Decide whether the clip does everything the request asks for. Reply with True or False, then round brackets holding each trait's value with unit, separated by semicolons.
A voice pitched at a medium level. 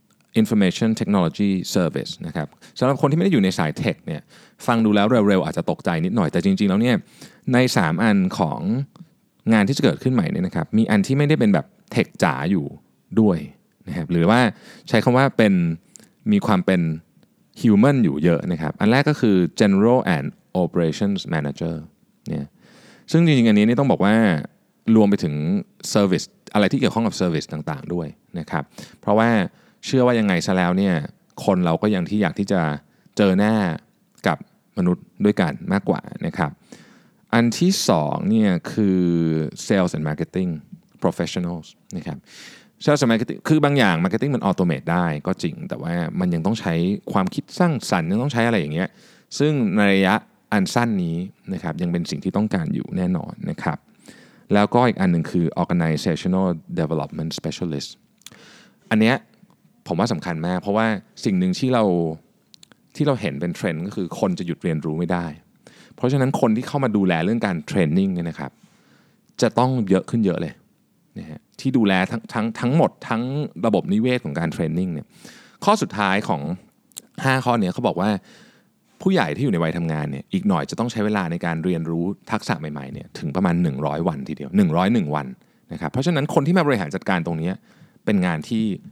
False (110 Hz)